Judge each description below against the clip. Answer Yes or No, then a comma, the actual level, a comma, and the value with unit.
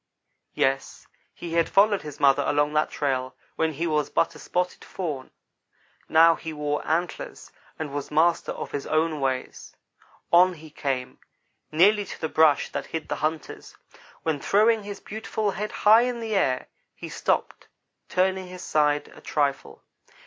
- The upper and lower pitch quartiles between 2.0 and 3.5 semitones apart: No, average, 4.0 semitones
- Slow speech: No, average, 160 wpm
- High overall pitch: No, medium, 160 Hz